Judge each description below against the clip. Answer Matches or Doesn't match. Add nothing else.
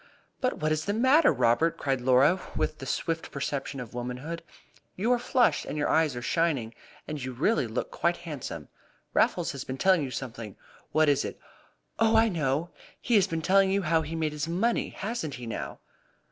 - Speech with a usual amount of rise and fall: Doesn't match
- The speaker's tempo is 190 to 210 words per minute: Matches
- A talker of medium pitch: Matches